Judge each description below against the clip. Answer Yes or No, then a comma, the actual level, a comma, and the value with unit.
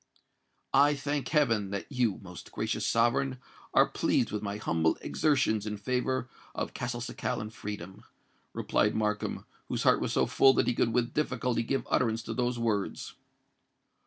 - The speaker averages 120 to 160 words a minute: Yes, average, 155 wpm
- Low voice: Yes, low, 115 Hz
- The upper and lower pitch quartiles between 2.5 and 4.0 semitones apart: Yes, average, 3.5 semitones